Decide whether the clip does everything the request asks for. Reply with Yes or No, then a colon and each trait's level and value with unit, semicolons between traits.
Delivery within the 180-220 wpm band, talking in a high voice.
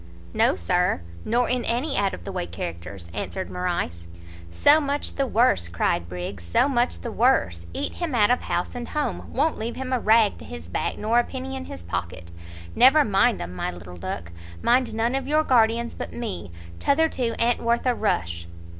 Yes: average, 200 wpm; high, 220 Hz